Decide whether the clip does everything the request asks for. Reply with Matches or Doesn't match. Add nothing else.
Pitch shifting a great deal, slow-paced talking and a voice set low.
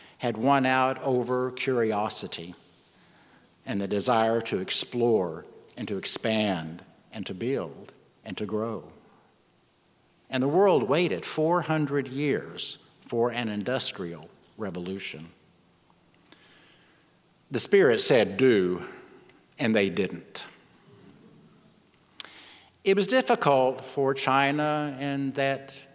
Doesn't match